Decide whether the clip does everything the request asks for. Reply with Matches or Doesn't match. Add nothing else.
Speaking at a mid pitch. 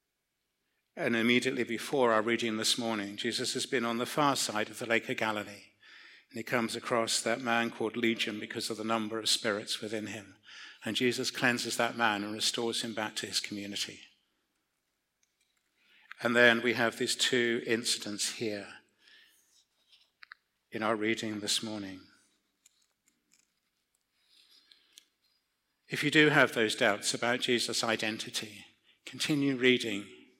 Doesn't match